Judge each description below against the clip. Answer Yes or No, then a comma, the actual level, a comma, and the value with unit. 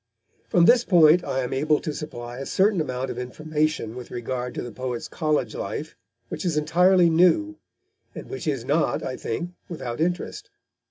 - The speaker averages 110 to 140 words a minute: No, average, 175 wpm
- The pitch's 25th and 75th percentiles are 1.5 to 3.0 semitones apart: No, wide, 5.5 semitones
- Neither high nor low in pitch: Yes, medium, 150 Hz